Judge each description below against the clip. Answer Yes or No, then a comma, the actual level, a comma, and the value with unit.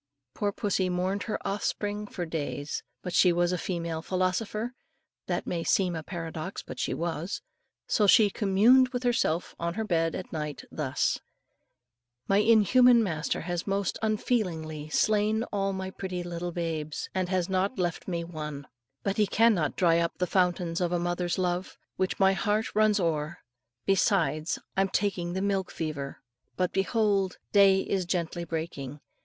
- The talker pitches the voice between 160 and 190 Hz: Yes, medium, 185 Hz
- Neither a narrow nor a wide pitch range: Yes, average, 3.2 semitones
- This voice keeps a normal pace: Yes, average, 165 wpm